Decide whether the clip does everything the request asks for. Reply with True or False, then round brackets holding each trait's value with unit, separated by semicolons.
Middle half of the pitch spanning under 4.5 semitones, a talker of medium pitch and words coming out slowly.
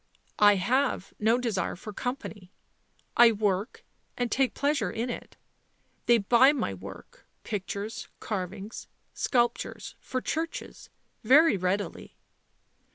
False (4.0 semitones; 220 Hz; 120 wpm)